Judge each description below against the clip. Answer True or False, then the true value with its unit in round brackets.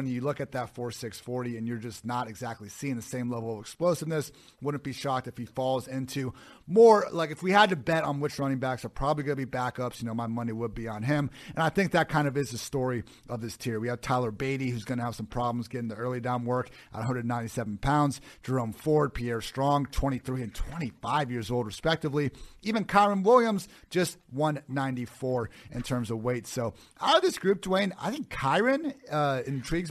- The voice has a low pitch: True (130 Hz)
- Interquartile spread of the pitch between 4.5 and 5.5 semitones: False (3.7 semitones)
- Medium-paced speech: False (215 wpm)